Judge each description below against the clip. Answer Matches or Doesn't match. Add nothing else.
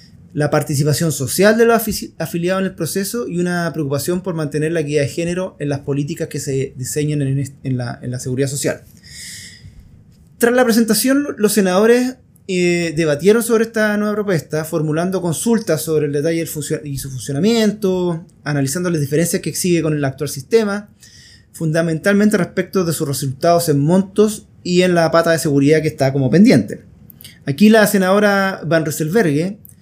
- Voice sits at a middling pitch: Matches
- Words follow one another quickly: Doesn't match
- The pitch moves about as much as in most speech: Matches